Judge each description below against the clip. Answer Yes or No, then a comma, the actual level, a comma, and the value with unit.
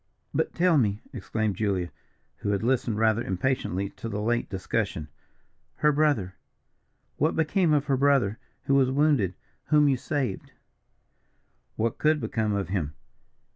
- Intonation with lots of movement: Yes, wide, 6.2 semitones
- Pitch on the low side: Yes, low, 115 Hz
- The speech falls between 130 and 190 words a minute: Yes, average, 140 wpm